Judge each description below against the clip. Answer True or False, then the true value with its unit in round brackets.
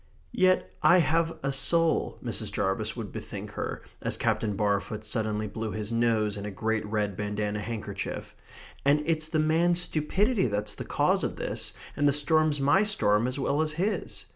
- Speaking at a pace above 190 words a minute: False (175 wpm)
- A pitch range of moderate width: False (7.0 semitones)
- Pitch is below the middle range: True (120 Hz)